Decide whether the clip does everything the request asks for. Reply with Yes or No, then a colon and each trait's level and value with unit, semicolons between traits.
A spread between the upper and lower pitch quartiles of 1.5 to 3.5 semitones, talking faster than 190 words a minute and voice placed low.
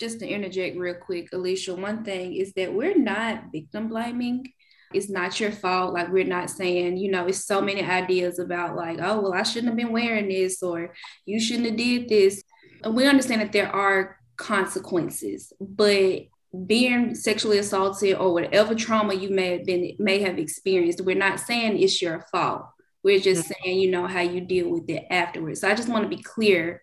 No: average, 3.1 semitones; average, 200 wpm; high, 195 Hz